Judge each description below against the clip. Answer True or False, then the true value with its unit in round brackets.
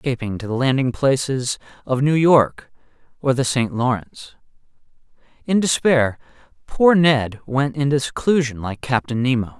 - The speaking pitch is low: True (130 Hz)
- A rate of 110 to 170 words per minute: True (140 wpm)